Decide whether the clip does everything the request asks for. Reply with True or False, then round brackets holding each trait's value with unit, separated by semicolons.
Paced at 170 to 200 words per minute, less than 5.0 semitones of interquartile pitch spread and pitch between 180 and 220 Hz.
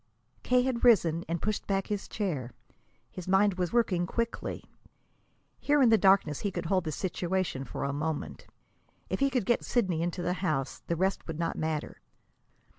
True (180 wpm; 4.1 semitones; 185 Hz)